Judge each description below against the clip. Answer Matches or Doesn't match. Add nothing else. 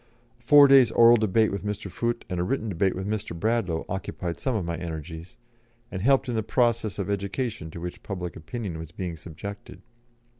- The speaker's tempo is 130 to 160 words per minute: Doesn't match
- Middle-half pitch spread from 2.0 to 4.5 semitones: Doesn't match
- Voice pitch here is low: Matches